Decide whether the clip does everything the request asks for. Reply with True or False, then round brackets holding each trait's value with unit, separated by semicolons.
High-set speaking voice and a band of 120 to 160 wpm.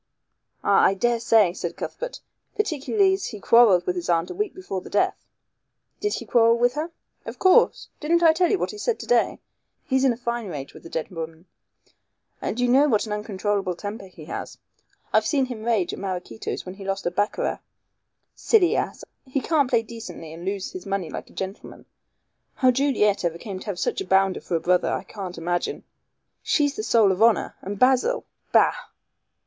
False (215 Hz; 200 wpm)